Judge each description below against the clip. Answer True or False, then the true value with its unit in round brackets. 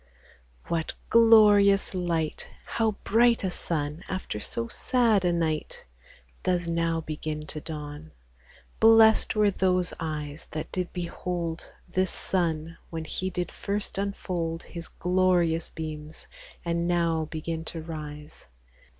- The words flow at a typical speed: False (125 wpm)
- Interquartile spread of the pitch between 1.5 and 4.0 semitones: True (2.9 semitones)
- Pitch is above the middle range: False (170 Hz)